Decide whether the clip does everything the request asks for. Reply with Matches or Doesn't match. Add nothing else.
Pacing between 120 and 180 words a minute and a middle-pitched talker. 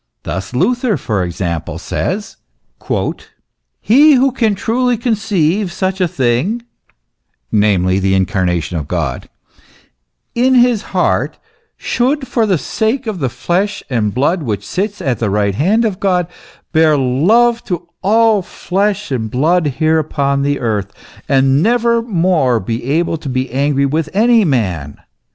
Matches